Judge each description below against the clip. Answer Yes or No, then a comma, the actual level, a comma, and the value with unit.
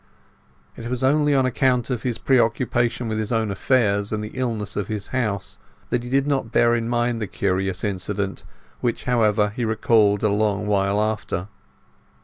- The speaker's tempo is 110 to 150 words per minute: No, average, 175 wpm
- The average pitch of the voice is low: Yes, low, 110 Hz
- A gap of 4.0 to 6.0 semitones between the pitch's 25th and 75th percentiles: No, average, 3.0 semitones